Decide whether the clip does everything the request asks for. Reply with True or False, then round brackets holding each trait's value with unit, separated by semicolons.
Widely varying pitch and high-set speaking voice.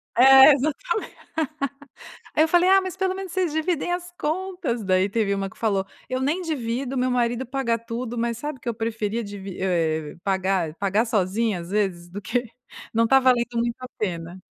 True (6.1 semitones; 235 Hz)